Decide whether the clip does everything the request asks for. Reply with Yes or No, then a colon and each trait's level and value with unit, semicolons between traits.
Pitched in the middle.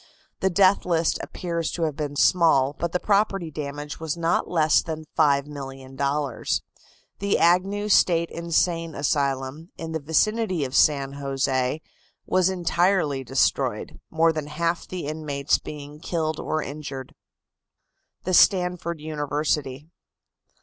Yes: medium, 155 Hz